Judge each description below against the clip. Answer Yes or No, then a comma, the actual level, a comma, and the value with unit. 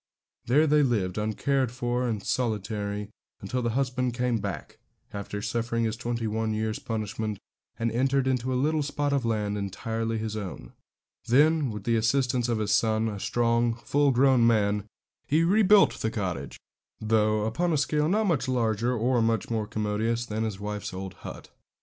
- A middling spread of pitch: Yes, average, 3.1 semitones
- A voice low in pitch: Yes, low, 115 Hz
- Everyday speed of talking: Yes, average, 175 wpm